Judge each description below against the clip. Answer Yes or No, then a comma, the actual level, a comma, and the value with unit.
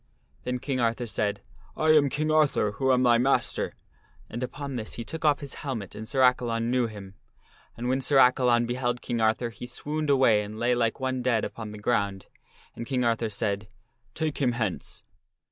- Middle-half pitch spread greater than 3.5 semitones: No, average, 2.7 semitones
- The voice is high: No, low, 120 Hz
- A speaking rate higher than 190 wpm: Yes, average, 200 wpm